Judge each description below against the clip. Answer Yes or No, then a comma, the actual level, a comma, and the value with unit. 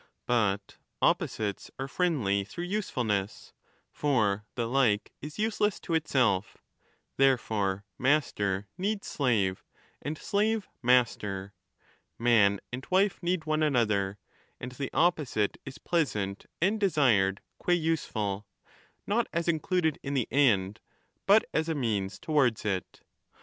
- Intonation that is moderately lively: No, wide, 7.8 semitones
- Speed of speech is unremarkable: No, slow, 125 wpm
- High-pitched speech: No, low, 125 Hz